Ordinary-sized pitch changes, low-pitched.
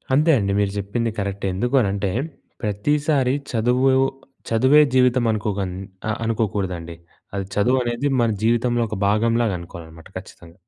Yes: average, 3.7 semitones; low, 110 Hz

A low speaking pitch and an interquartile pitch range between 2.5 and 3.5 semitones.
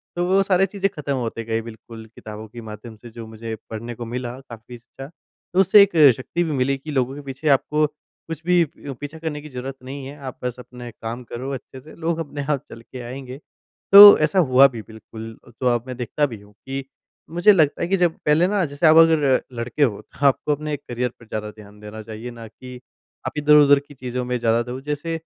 No: low, 130 Hz; average, 4.5 semitones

